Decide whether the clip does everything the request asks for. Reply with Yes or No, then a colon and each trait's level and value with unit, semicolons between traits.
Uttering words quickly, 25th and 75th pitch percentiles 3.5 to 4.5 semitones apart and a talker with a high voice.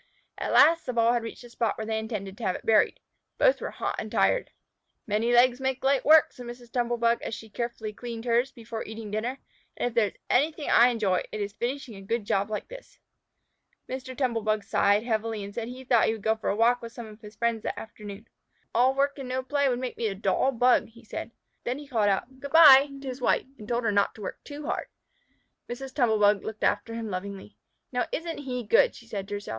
No: fast, 240 wpm; average, 3.1 semitones; high, 235 Hz